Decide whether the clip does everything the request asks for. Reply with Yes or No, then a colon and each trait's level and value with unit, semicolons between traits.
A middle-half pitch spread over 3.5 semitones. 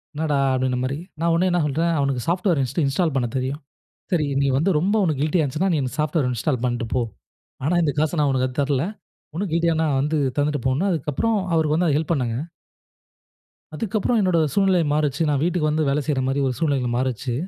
Yes: average, 4.0 semitones